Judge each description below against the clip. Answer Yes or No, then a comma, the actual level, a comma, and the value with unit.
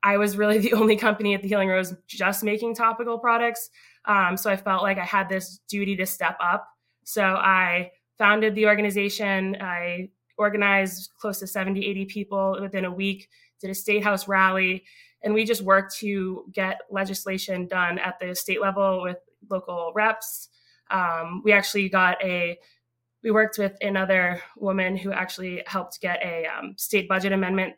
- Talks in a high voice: Yes, high, 195 Hz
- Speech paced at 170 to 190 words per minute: Yes, average, 175 wpm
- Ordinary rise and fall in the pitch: No, narrow, 1.8 semitones